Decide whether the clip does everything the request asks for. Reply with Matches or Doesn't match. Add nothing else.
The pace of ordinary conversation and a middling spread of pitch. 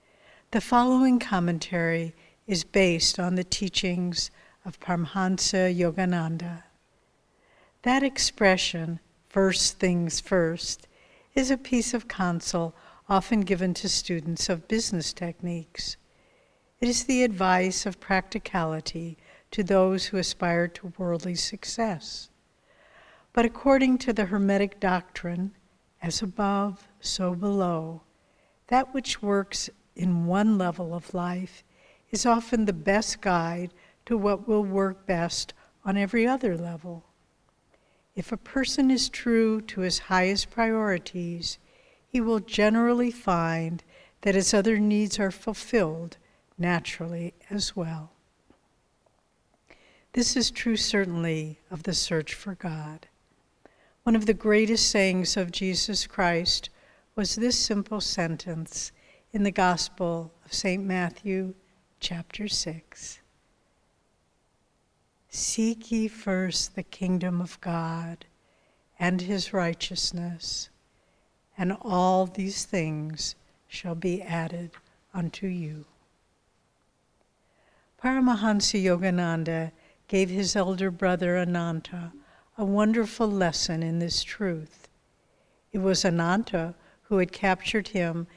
Doesn't match